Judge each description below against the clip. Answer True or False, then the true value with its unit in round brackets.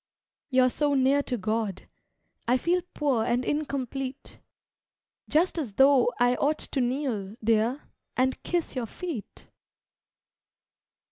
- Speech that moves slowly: True (120 wpm)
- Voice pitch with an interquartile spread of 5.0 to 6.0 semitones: False (3.2 semitones)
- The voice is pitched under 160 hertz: False (260 Hz)